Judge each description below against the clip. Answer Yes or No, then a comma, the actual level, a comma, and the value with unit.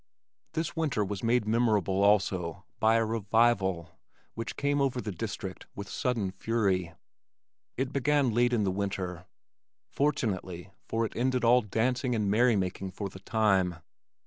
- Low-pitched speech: Yes, low, 110 Hz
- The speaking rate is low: No, average, 145 wpm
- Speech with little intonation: No, average, 4.2 semitones